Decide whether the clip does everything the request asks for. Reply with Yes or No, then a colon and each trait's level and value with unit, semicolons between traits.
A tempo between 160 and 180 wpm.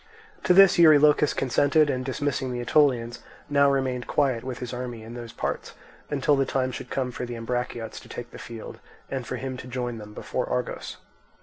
No: average, 195 wpm